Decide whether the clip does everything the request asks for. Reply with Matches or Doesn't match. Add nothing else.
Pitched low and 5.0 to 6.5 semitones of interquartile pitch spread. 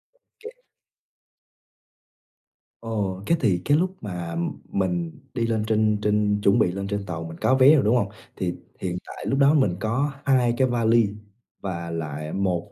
Matches